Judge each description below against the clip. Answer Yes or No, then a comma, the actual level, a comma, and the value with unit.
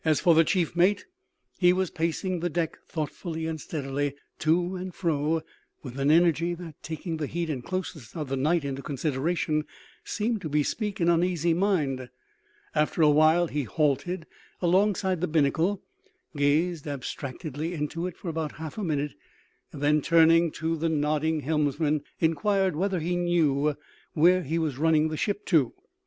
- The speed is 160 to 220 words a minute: Yes, average, 165 wpm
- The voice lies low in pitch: No, medium, 160 Hz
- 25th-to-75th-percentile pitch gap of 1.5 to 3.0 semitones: Yes, average, 2.7 semitones